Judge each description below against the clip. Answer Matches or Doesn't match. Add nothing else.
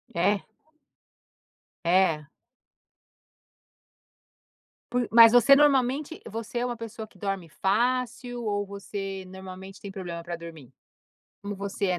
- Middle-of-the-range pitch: Doesn't match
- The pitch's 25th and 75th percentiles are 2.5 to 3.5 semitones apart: Doesn't match